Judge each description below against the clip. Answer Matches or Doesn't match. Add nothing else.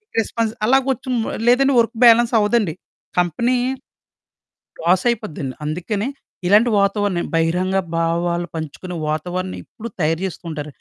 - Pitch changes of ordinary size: Doesn't match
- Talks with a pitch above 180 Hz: Matches